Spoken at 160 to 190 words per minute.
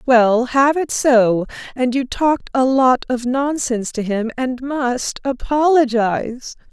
No: average, 145 wpm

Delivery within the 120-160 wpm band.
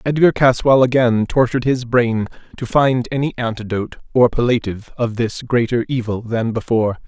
Yes: average, 155 wpm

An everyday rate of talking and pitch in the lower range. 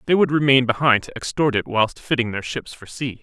No: fast, 240 wpm; low, 125 Hz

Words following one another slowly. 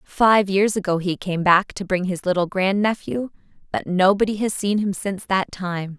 No: average, 200 wpm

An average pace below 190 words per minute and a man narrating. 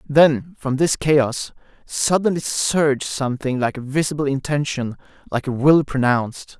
Yes: slow, 135 wpm; male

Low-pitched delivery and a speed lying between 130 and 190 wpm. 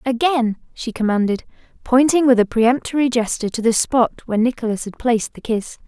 No: high, 235 Hz; average, 175 wpm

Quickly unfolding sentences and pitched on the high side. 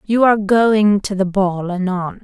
No: average, 190 wpm; high, 200 Hz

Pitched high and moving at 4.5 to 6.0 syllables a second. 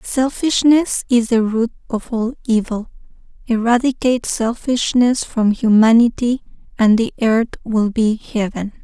No: high, 230 Hz; 4.3 syllables/s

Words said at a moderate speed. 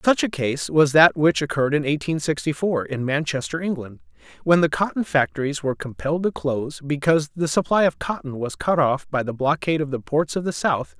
No: fast, 235 wpm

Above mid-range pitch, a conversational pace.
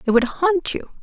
No: very high, 305 Hz; fast, 235 wpm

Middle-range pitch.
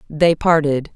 Yes: medium, 155 Hz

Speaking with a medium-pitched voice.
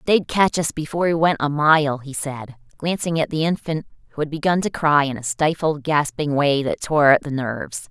Yes: medium, 150 Hz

